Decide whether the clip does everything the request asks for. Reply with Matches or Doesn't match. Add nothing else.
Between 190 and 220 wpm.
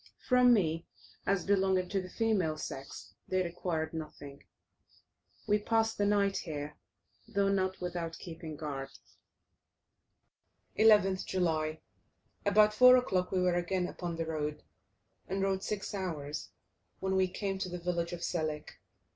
Doesn't match